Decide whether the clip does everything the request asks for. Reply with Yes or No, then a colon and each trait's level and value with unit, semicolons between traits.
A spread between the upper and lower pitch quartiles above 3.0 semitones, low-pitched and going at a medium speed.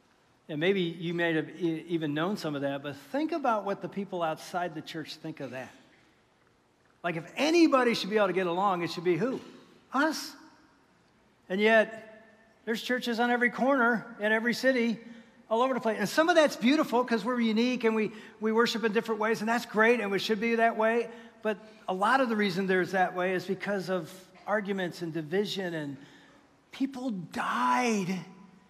No: average, 4.6 semitones; high, 215 Hz; average, 190 wpm